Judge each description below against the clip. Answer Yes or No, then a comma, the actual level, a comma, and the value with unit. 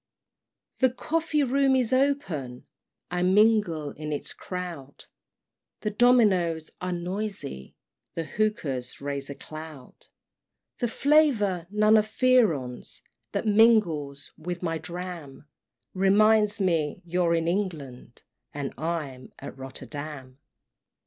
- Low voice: No, medium, 175 Hz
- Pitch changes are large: Yes, wide, 6.5 semitones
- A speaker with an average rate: No, slow, 110 wpm